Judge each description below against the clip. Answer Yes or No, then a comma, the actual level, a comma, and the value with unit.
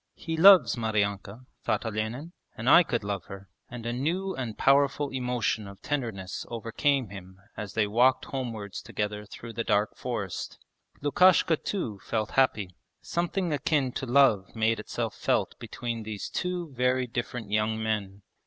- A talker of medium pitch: No, low, 115 Hz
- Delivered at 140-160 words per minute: Yes, average, 155 wpm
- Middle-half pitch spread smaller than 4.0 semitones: No, average, 4.6 semitones